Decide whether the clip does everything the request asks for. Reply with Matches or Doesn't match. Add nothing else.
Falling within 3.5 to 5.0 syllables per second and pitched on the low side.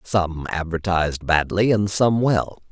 Matches